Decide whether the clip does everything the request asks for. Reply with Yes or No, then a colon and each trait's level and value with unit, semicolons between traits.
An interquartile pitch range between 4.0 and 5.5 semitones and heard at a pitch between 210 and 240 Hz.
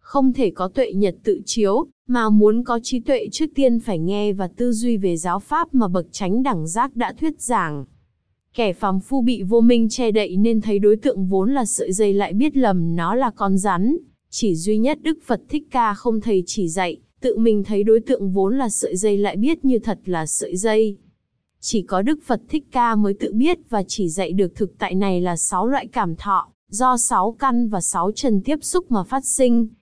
Yes: average, 4.7 semitones; high, 220 Hz